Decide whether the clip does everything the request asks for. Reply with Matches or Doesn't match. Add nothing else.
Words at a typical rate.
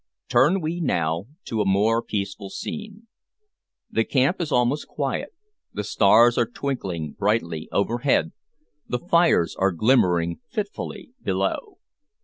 Doesn't match